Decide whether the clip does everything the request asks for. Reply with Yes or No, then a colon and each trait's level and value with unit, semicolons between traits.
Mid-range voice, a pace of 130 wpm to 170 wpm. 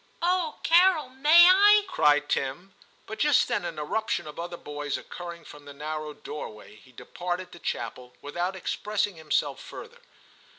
Yes: medium, 175 Hz; average, 165 wpm